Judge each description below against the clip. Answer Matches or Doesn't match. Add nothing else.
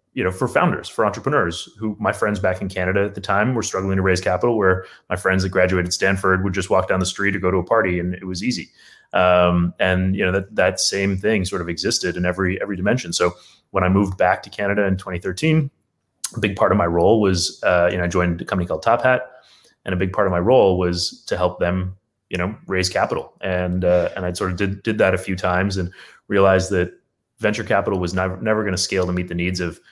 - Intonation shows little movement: Matches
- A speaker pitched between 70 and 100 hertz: Matches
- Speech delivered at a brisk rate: Matches